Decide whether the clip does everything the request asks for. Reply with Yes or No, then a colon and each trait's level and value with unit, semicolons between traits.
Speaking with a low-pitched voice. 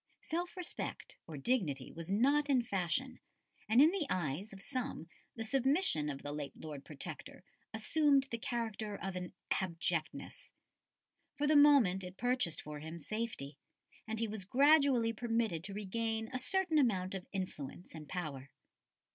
No: high, 215 Hz